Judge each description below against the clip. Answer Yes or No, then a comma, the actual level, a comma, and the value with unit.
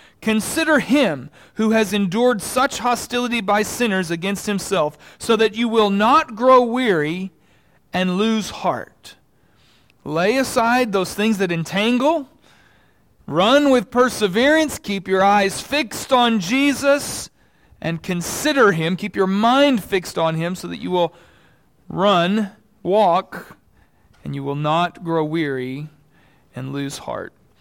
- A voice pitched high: Yes, high, 205 Hz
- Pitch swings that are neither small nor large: No, wide, 6.2 semitones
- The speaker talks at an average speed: No, slow, 130 wpm